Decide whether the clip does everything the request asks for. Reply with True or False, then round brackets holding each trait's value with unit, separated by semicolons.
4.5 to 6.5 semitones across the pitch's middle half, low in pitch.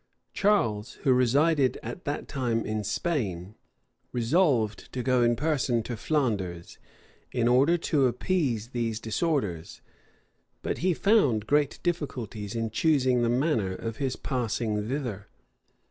True (4.9 semitones; 125 Hz)